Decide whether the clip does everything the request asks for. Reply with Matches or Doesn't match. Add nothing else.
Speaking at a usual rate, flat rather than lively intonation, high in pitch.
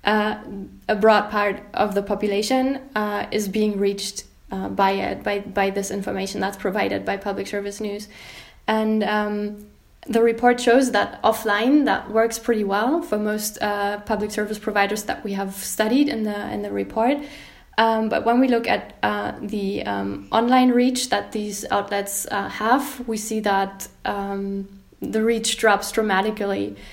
Matches